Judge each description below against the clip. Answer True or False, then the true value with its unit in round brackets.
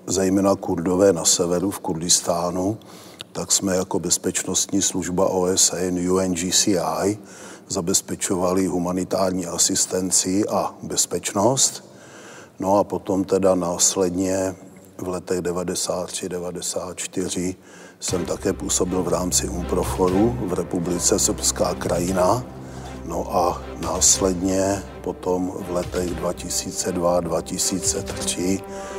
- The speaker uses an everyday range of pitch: False (1.2 semitones)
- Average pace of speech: False (95 wpm)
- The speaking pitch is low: True (90 Hz)